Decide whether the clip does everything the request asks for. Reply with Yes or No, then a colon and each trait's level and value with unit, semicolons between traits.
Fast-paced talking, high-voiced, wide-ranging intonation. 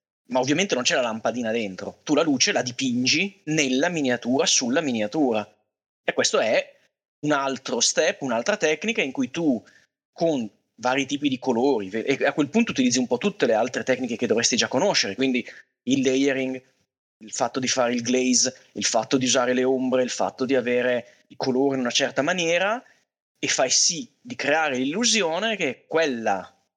No: fast, 180 wpm; low, 135 Hz; wide, 8.4 semitones